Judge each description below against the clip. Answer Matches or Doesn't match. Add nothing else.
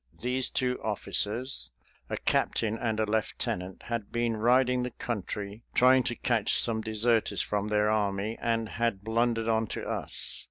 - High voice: Doesn't match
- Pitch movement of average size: Doesn't match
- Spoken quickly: Doesn't match